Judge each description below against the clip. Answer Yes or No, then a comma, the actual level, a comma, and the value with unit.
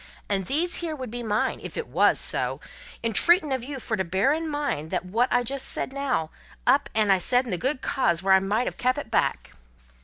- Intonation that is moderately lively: No, wide, 6.0 semitones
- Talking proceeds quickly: Yes, fast, 235 wpm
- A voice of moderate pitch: No, high, 245 Hz